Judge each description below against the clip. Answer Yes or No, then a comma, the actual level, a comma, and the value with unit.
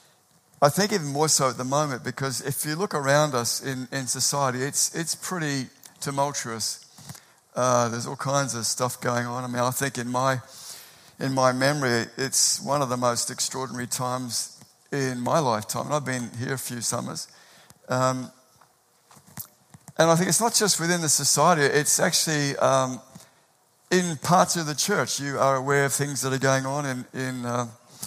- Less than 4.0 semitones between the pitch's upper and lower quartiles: Yes, average, 3.0 semitones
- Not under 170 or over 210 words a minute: Yes, average, 180 wpm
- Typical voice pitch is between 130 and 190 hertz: Yes, low, 135 Hz